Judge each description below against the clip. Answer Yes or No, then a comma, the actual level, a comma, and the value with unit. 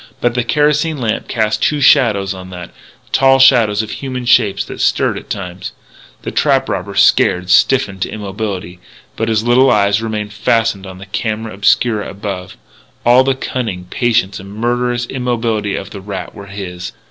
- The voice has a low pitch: Yes, low, 110 Hz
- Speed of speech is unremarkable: Yes, average, 170 wpm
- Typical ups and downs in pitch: Yes, average, 3.8 semitones